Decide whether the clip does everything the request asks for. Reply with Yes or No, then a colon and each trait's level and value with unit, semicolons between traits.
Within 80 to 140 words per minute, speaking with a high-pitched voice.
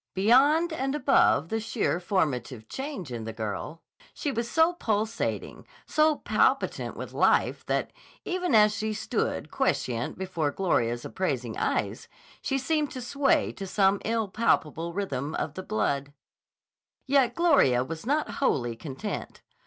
Yes: slow, 135 wpm; high, 200 Hz